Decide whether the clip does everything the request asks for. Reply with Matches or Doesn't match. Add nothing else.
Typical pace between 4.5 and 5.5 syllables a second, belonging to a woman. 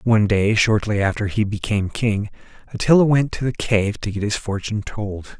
Doesn't match